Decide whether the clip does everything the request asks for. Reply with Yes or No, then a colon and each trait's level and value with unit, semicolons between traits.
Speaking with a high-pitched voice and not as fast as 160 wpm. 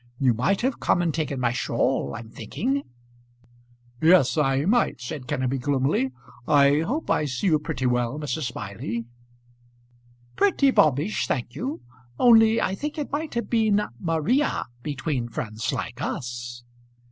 No: medium, 145 Hz; average, 145 wpm